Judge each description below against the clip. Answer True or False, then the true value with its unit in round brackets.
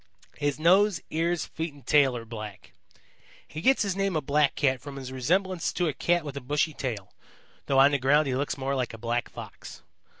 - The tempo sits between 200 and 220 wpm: True (205 wpm)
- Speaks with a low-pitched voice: False (145 Hz)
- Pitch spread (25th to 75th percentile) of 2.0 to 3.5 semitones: False (3.9 semitones)